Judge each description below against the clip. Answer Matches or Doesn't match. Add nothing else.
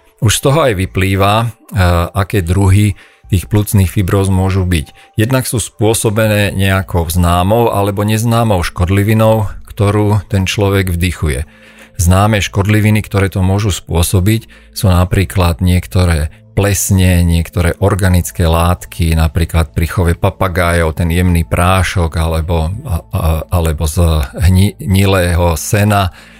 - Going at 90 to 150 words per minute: Matches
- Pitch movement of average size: Matches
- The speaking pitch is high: Doesn't match